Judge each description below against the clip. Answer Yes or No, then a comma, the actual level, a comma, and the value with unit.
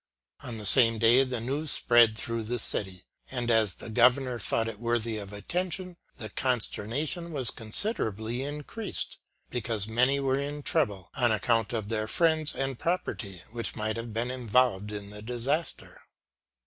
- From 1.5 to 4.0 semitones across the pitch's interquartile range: Yes, average, 3.7 semitones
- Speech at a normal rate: Yes, average, 160 wpm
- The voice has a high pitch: No, low, 120 Hz